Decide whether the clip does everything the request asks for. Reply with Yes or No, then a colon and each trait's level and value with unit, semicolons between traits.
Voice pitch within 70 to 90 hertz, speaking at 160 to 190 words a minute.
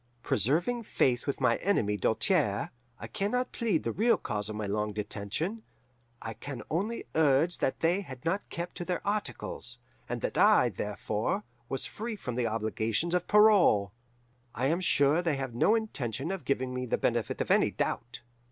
No: medium, 140 Hz; average, 180 wpm